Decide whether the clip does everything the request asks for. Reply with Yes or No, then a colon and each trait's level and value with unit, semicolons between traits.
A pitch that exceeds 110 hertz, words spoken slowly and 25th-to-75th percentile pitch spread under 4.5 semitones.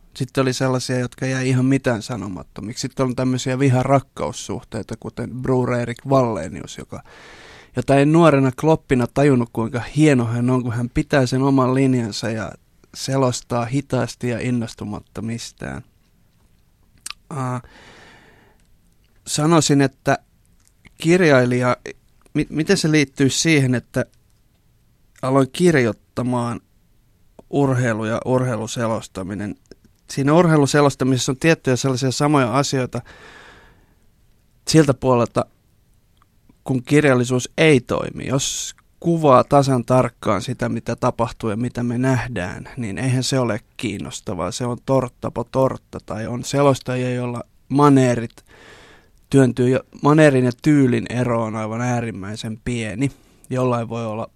No: low, 125 Hz; average, 105 wpm; average, 2.8 semitones